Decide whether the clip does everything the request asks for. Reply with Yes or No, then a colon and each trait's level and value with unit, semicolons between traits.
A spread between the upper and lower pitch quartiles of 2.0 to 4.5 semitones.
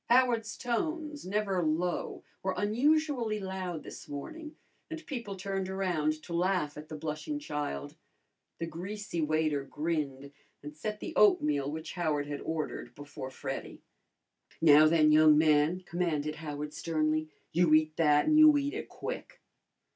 No: wide, 5.5 semitones